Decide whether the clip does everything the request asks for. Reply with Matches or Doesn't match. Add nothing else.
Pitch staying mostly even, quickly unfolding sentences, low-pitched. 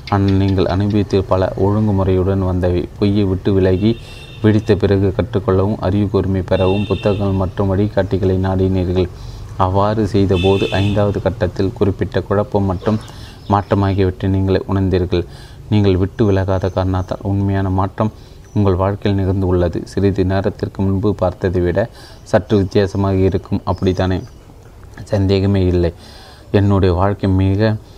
Doesn't match